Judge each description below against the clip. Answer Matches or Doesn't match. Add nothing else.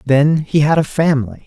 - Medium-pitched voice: Matches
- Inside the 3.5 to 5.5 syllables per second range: Matches